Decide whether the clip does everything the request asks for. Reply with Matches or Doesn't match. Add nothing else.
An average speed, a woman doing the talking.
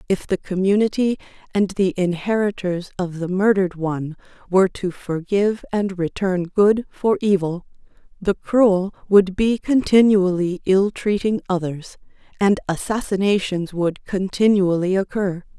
Doesn't match